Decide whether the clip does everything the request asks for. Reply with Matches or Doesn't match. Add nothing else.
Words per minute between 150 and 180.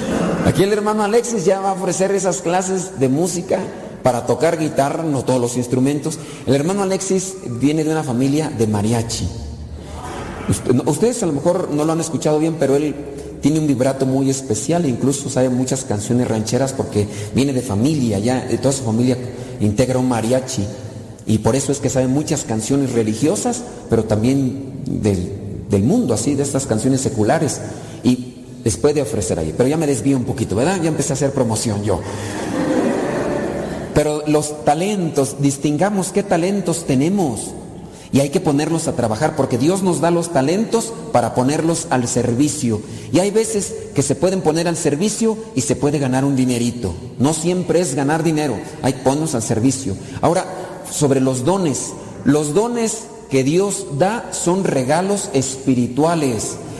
Matches